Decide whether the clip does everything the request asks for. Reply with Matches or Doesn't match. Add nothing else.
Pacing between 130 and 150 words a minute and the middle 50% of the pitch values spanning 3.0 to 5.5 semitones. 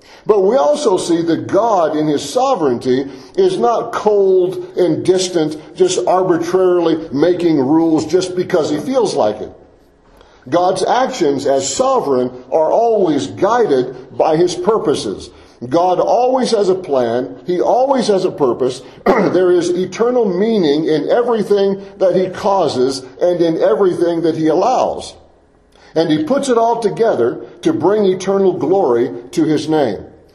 Matches